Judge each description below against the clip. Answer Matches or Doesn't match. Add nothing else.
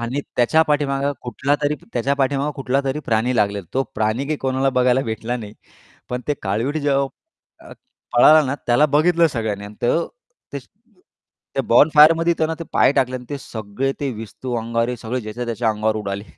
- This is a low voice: Matches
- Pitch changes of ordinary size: Matches